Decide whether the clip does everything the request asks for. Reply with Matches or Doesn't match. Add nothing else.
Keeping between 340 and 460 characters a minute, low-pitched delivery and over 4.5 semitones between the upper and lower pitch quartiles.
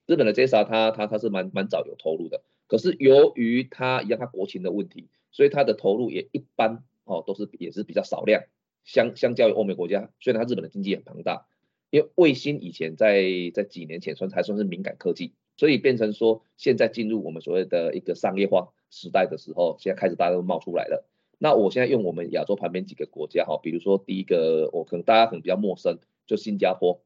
Matches